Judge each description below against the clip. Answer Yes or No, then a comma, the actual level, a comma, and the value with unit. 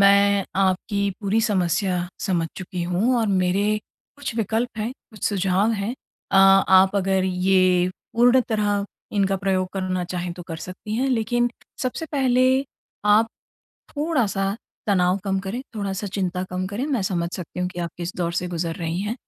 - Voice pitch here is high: Yes, high, 195 Hz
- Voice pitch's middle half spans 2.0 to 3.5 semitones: Yes, average, 2.9 semitones